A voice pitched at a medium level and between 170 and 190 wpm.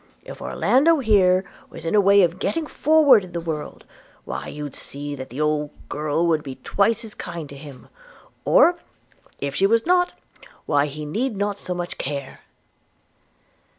Yes: medium, 175 Hz; average, 175 wpm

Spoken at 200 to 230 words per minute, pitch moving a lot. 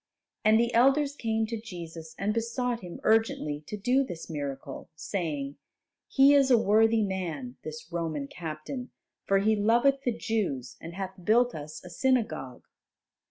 No: average, 155 wpm; wide, 6.6 semitones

